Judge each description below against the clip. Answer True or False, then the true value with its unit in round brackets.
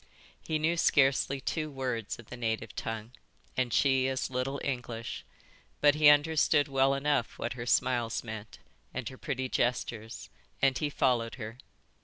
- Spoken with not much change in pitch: False (3.0 semitones)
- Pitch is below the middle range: True (130 Hz)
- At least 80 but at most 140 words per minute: False (155 wpm)